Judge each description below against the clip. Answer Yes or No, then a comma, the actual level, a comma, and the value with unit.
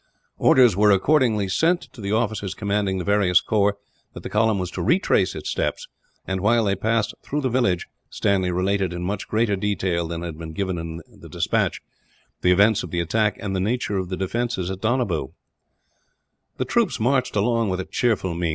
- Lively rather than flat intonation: No, average, 3.5 semitones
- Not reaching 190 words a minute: No, average, 195 wpm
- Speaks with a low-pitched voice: Yes, low, 100 Hz